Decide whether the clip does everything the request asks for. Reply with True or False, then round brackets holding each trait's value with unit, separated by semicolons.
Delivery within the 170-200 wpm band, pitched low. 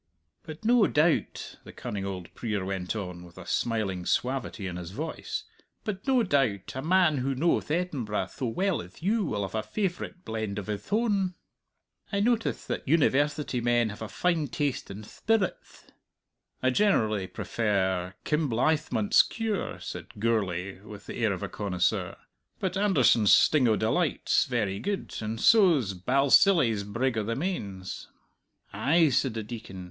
False (160 wpm; 125 Hz)